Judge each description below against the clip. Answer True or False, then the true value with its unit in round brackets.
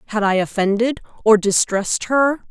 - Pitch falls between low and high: False (220 Hz)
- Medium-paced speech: True (145 wpm)